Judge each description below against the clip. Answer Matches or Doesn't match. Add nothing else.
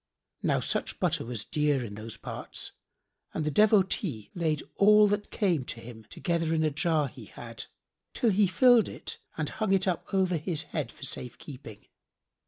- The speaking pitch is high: Doesn't match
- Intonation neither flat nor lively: Doesn't match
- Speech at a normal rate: Matches